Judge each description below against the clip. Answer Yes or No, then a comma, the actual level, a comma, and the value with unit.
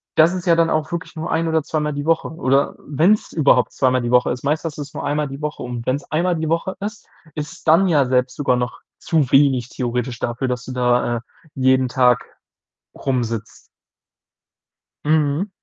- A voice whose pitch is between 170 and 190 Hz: No, medium, 145 Hz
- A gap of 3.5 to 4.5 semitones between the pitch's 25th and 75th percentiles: Yes, average, 4.2 semitones